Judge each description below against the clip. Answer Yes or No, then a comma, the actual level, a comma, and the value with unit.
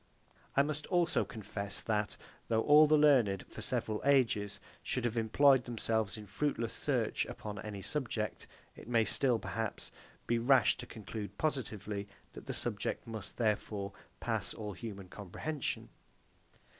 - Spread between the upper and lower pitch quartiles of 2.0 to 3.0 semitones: No, average, 4.4 semitones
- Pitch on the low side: Yes, low, 115 Hz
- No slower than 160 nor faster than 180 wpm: No, average, 145 wpm